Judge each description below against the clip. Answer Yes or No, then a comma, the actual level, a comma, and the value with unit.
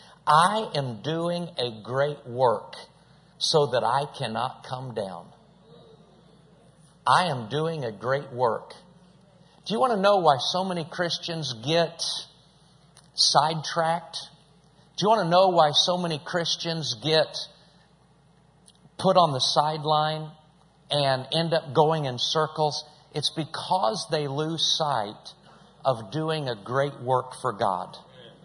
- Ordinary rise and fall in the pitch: Yes, average, 3.1 semitones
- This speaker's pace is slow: Yes, slow, 130 wpm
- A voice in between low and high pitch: Yes, medium, 155 Hz